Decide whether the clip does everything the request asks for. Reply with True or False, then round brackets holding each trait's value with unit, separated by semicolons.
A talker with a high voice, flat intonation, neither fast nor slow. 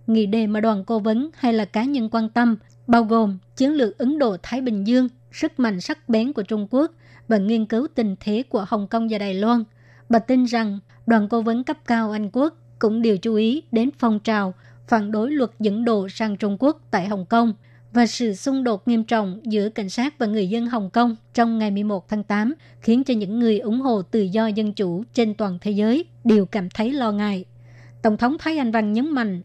True (225 Hz; 2.3 semitones; 225 wpm)